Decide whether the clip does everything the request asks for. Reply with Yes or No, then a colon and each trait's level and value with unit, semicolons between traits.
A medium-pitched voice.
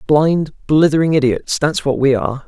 Yes: medium, 145 Hz